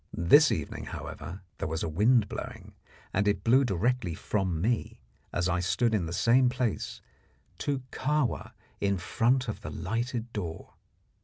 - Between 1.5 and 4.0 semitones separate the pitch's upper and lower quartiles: No, wide, 5.6 semitones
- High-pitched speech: No, low, 105 Hz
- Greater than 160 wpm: No, average, 155 wpm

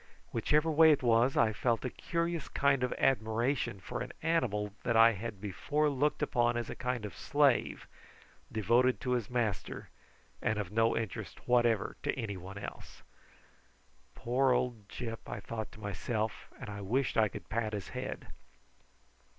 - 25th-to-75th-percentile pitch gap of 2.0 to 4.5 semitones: Yes, average, 3.1 semitones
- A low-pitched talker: Yes, low, 115 Hz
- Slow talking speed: No, average, 160 wpm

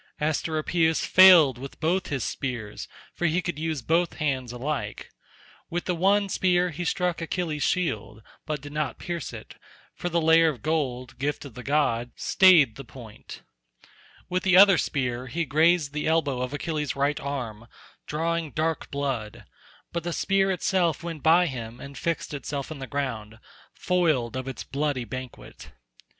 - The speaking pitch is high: No, medium, 150 Hz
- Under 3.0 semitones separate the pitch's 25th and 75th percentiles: No, average, 4.5 semitones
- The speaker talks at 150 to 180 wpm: Yes, average, 165 wpm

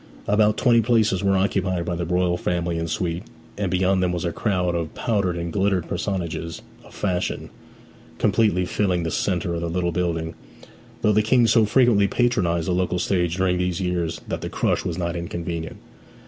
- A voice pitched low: Yes, very low, 90 Hz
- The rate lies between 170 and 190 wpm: Yes, average, 185 wpm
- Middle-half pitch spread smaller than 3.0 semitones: Yes, narrow, 2.6 semitones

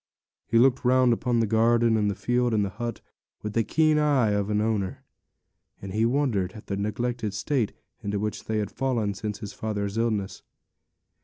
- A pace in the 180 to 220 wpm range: Yes, average, 185 wpm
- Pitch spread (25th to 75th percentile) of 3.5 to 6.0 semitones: No, average, 2.9 semitones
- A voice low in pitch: Yes, low, 110 Hz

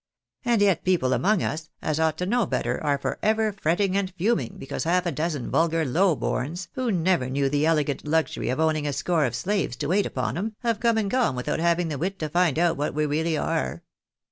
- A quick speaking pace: Yes, fast, 225 wpm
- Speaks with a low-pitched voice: No, medium, 165 Hz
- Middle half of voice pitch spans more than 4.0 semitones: Yes, average, 4.6 semitones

